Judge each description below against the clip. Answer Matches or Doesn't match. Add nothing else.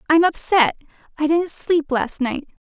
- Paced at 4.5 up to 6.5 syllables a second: Doesn't match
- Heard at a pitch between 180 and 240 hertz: Doesn't match